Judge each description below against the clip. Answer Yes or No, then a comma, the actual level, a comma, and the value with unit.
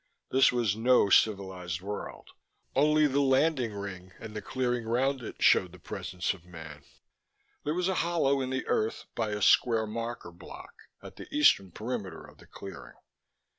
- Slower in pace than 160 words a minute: No, average, 170 wpm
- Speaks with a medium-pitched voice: No, low, 110 Hz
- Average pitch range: No, wide, 5.8 semitones